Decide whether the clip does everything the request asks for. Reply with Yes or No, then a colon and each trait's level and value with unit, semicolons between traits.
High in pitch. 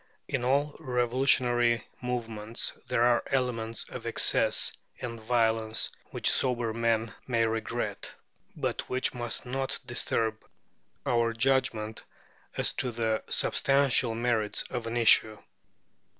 No: low, 120 Hz